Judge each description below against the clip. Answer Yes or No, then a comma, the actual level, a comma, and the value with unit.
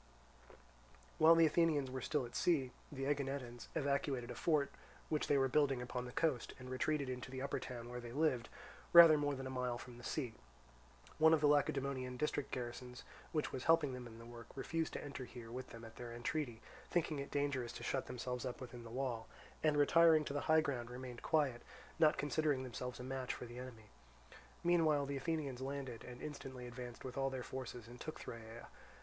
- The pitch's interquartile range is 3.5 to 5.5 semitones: No, average, 3.1 semitones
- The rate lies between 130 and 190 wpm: No, fast, 205 wpm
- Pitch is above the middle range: No, low, 130 Hz